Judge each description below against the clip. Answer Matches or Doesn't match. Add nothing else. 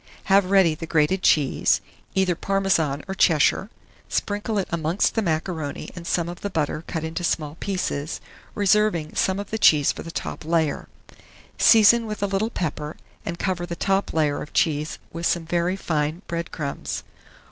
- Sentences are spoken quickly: Doesn't match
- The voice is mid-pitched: Matches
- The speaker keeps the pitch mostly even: Doesn't match